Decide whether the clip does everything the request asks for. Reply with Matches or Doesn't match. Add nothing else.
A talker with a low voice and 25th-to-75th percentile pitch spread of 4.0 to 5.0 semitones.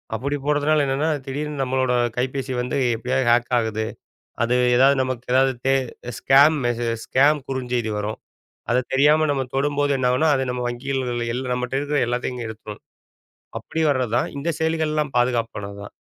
Doesn't match